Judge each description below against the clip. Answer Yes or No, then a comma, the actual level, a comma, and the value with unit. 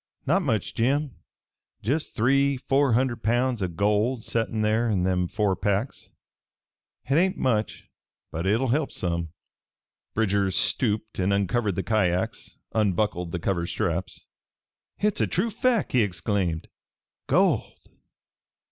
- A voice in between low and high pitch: No, low, 110 Hz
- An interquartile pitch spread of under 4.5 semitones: No, average, 5.3 semitones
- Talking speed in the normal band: No, slow, 130 wpm